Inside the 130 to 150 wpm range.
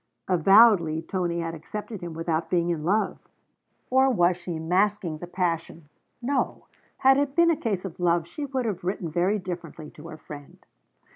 No: average, 170 wpm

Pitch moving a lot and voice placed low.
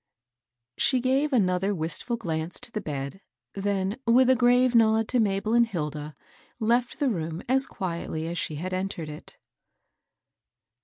No: wide, 6.3 semitones; high, 200 Hz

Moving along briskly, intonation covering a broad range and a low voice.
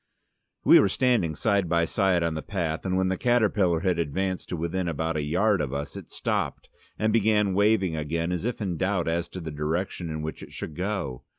No: fast, 215 wpm; average, 3.5 semitones; very low, 90 Hz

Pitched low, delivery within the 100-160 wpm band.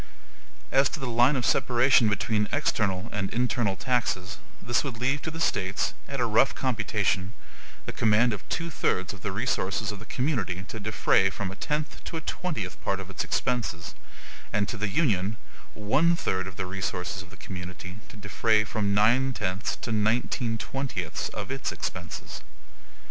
No: low, 110 Hz; average, 175 wpm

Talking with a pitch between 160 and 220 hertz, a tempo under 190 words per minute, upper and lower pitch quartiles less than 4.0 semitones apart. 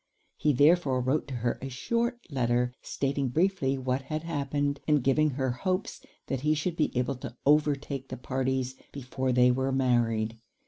No: low, 135 Hz; average, 170 wpm; average, 2.9 semitones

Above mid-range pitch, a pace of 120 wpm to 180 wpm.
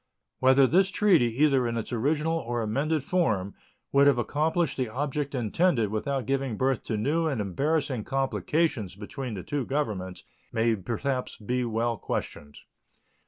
No: low, 130 Hz; average, 150 wpm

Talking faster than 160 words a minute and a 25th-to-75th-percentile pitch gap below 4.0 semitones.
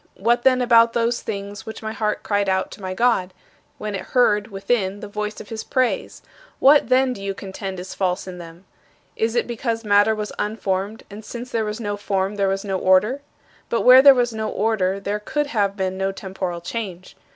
Yes: fast, 205 wpm; average, 3.1 semitones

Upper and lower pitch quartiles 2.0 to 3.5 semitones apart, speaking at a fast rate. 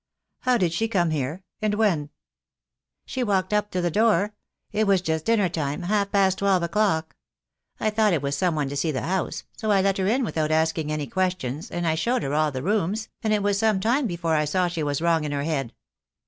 No: average, 4.9 semitones; fast, 240 wpm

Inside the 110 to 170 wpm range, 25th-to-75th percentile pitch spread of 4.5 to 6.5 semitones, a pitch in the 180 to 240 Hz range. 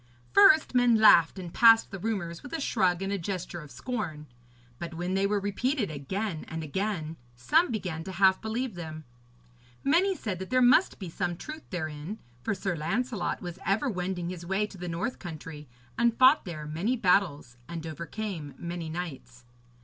No: average, 180 wpm; average, 5.1 semitones; medium, 185 Hz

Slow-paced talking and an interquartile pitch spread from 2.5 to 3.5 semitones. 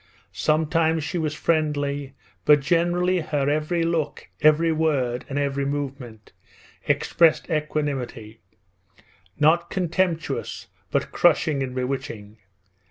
Yes: slow, 100 wpm; average, 3.0 semitones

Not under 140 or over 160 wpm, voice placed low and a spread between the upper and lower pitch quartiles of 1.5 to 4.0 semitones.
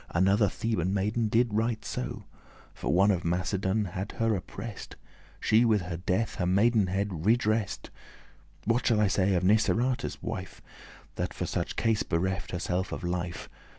Yes: average, 155 wpm; low, 100 Hz; average, 3.3 semitones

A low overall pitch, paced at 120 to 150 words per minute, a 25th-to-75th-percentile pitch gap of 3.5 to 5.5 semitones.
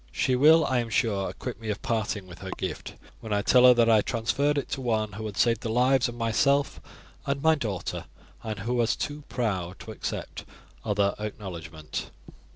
No: low, 115 Hz; average, 195 wpm; average, 3.8 semitones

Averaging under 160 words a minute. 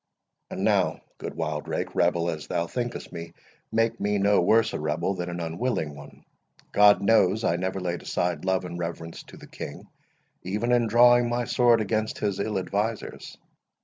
No: average, 175 wpm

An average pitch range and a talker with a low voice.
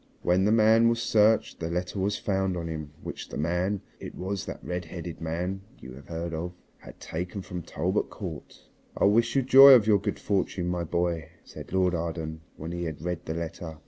Yes: average, 3.4 semitones; very low, 90 Hz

